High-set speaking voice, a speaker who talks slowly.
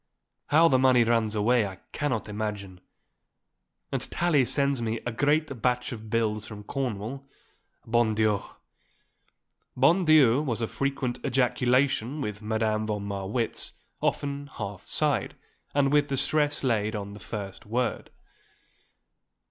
No: low, 120 Hz; slow, 130 wpm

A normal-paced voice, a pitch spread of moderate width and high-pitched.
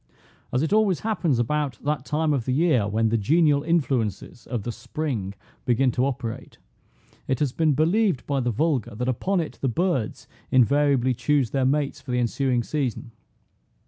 No: average, 175 wpm; average, 4.0 semitones; low, 135 Hz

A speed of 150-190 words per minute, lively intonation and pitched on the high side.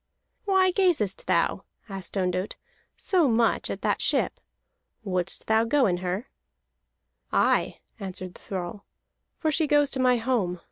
No: average, 140 wpm; wide, 7.8 semitones; high, 220 Hz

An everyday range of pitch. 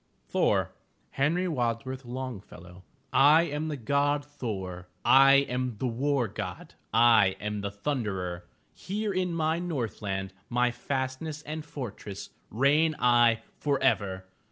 No: wide, 5.7 semitones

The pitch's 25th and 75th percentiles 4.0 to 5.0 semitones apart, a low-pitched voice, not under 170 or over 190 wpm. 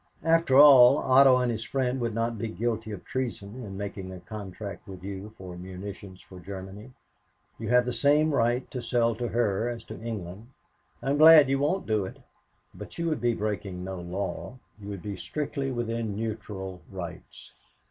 Yes: average, 4.3 semitones; low, 115 Hz; average, 180 wpm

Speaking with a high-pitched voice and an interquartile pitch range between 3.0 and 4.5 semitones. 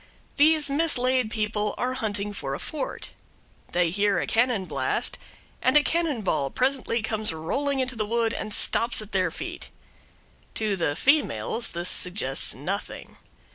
No: high, 220 Hz; average, 5.1 semitones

